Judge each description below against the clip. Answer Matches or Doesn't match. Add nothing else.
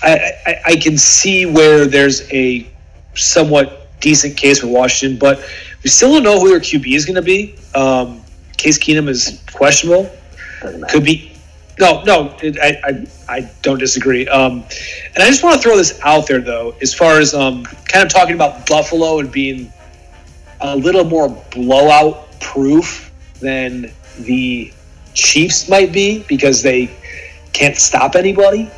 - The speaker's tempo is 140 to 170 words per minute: Matches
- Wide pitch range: Doesn't match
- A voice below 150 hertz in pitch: Matches